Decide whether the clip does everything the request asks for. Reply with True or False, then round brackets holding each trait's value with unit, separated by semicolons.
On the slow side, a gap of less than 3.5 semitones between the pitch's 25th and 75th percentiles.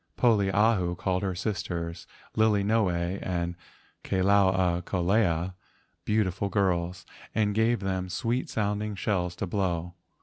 True (115 wpm; 2.9 semitones)